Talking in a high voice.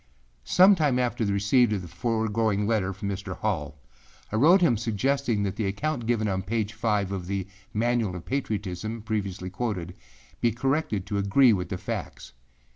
No: low, 105 Hz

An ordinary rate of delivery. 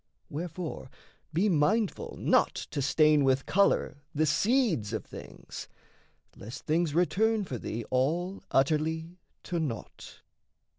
No: slow, 115 wpm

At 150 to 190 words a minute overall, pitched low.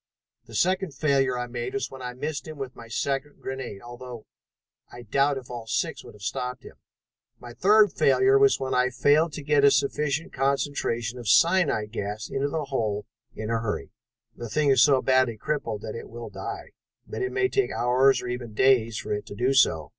No: fast, 205 wpm; low, 130 Hz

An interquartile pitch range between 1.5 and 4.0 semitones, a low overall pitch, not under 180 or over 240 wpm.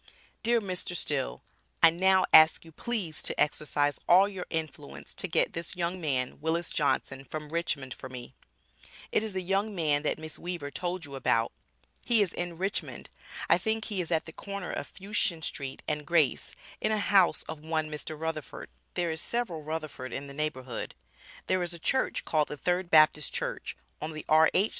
No: average, 3.6 semitones; medium, 160 Hz; average, 185 wpm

